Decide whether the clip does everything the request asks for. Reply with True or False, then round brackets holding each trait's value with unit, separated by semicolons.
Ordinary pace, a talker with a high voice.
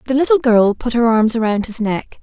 False (245 wpm; 235 Hz)